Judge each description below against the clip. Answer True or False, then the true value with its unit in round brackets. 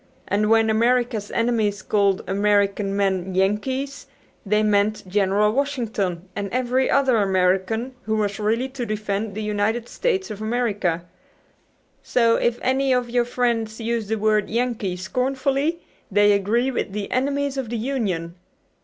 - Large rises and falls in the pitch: False (3.5 semitones)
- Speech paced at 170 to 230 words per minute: False (145 wpm)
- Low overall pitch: False (220 Hz)